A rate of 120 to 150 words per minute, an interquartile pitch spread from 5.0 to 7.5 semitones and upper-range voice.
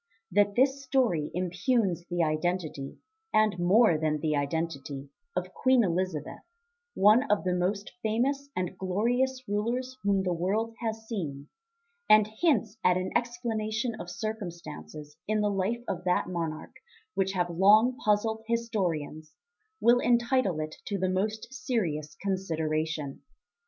Yes: slow, 135 wpm; average, 5.3 semitones; high, 195 Hz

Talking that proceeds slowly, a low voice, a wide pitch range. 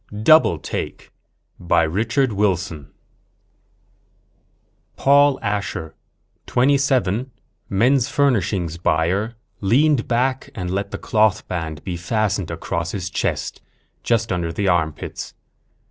Yes: slow, 120 wpm; low, 100 Hz; wide, 6.0 semitones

